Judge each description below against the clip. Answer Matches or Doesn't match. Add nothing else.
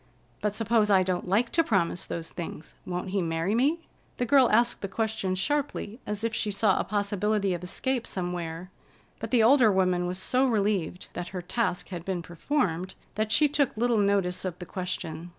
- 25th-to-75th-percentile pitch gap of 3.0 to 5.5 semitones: Matches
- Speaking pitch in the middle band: Doesn't match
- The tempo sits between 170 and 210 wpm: Matches